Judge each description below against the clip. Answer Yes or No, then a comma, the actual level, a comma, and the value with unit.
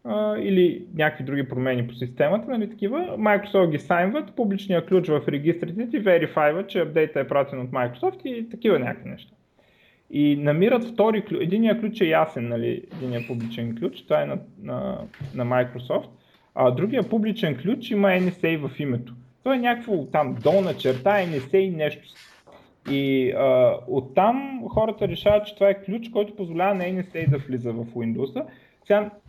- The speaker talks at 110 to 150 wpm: No, fast, 165 wpm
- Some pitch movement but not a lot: No, wide, 6.9 semitones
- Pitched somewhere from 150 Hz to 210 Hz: Yes, medium, 185 Hz